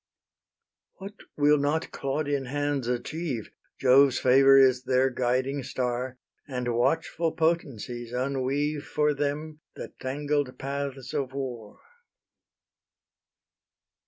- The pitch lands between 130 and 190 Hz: Yes, low, 135 Hz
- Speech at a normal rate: No, slow, 100 wpm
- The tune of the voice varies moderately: No, narrow, 2.3 semitones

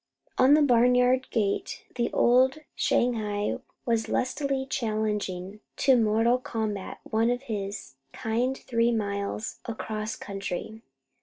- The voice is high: Yes, high, 225 Hz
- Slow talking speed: Yes, slow, 110 wpm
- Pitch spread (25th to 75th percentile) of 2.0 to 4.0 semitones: Yes, average, 2.9 semitones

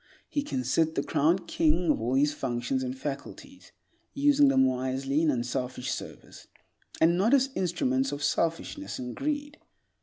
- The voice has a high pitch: No, medium, 145 Hz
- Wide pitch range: Yes, wide, 6.6 semitones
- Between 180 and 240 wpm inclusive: No, average, 155 wpm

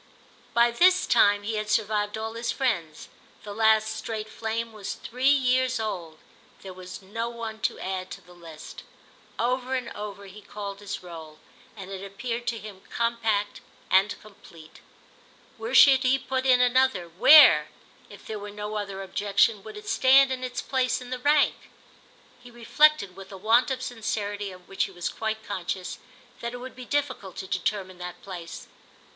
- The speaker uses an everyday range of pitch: Yes, average, 4.1 semitones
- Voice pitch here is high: Yes, high, 215 Hz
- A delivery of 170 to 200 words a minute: Yes, average, 175 wpm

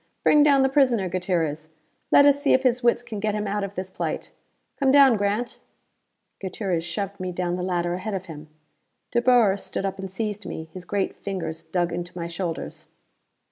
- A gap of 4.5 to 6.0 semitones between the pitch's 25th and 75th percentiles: Yes, average, 4.8 semitones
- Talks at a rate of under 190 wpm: No, average, 195 wpm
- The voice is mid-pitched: No, high, 195 Hz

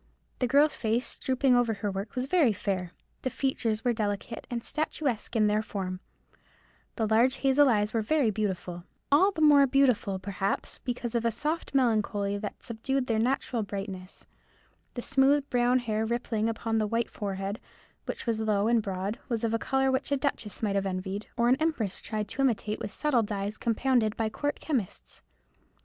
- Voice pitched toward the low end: No, high, 225 Hz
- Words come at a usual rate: Yes, average, 180 wpm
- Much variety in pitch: No, average, 4.1 semitones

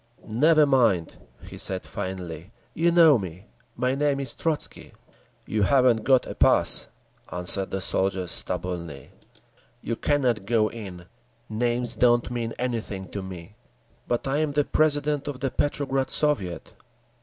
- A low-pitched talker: Yes, low, 120 Hz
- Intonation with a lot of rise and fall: Yes, wide, 6.5 semitones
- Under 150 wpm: Yes, average, 140 wpm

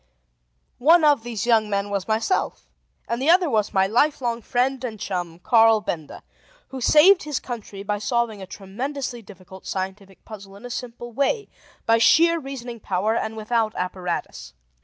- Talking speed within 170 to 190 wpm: No, average, 160 wpm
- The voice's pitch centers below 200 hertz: No, high, 225 Hz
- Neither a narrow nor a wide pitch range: Yes, average, 4.4 semitones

